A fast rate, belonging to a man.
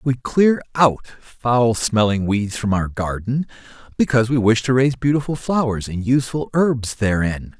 No: average, 160 wpm; male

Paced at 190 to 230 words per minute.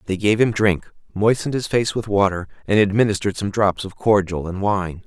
Yes: average, 200 wpm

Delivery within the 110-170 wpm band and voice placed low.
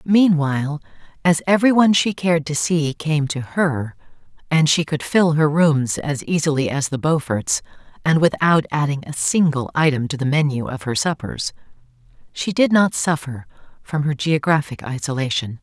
No: average, 160 wpm; medium, 150 Hz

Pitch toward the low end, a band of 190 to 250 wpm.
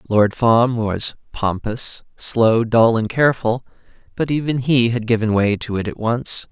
No: low, 115 Hz; average, 165 wpm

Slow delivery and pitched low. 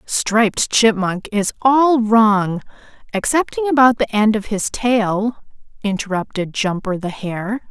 No: slow, 125 wpm; high, 220 Hz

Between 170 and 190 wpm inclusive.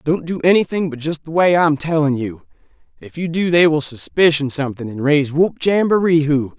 No: average, 200 wpm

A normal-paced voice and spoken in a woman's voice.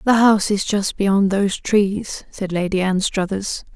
Yes: average, 160 wpm; female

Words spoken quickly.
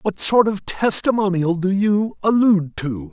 No: average, 155 wpm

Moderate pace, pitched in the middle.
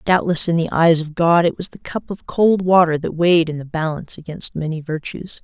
No: fast, 230 wpm; medium, 165 Hz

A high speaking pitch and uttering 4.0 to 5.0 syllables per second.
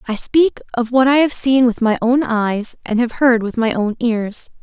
Yes: high, 240 Hz; 4.4 syllables/s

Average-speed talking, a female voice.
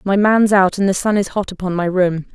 No: fast, 280 wpm; female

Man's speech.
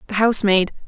No: female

